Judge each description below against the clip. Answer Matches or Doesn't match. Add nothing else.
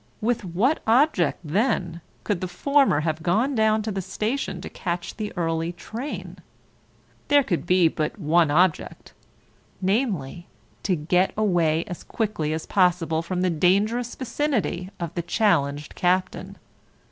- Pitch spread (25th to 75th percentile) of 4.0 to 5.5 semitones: Matches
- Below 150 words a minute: Matches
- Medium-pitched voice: Matches